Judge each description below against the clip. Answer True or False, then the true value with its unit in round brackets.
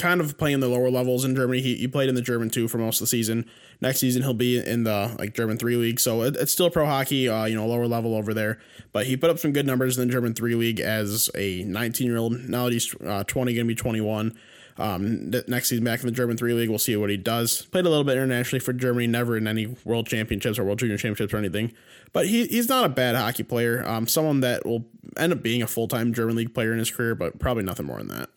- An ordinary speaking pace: False (275 wpm)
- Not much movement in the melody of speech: True (2.1 semitones)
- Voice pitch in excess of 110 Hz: True (120 Hz)